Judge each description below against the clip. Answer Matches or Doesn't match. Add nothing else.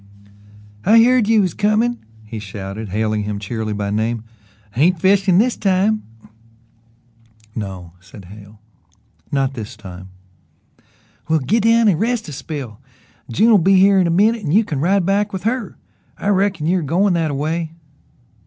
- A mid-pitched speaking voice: Matches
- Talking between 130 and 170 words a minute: Matches